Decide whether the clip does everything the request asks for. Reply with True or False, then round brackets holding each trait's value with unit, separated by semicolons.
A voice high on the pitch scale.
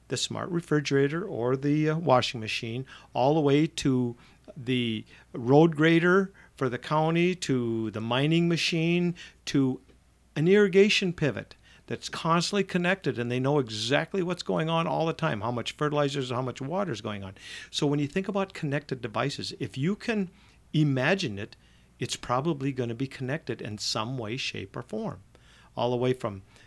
False (140 Hz)